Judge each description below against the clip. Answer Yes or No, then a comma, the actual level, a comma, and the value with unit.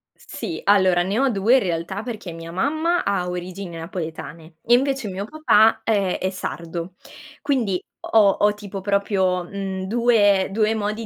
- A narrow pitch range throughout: No, average, 3.6 semitones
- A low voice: No, high, 200 Hz